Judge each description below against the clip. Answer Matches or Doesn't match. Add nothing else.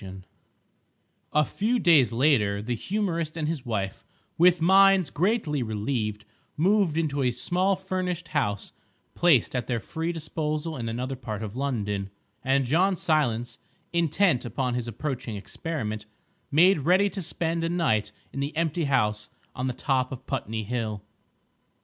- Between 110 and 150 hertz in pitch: Matches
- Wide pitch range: Matches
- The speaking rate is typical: Matches